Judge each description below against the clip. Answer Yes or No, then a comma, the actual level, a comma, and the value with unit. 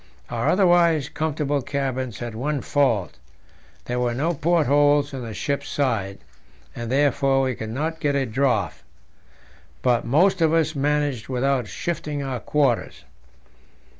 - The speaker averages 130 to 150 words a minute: Yes, slow, 135 wpm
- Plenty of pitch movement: No, average, 3.3 semitones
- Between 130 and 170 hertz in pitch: Yes, medium, 140 Hz